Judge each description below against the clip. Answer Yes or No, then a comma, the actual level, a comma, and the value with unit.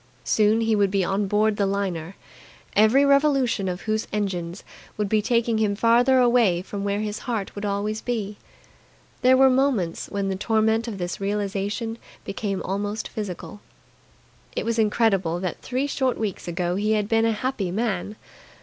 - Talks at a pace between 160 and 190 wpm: Yes, average, 170 wpm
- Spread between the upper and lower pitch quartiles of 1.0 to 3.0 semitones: Yes, narrow, 2.6 semitones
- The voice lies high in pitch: Yes, high, 210 Hz